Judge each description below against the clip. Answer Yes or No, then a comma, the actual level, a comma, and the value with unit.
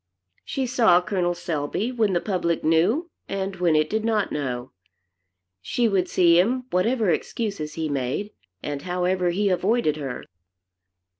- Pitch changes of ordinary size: Yes, average, 4.8 semitones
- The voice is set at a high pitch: No, medium, 180 Hz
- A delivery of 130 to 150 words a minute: Yes, average, 145 wpm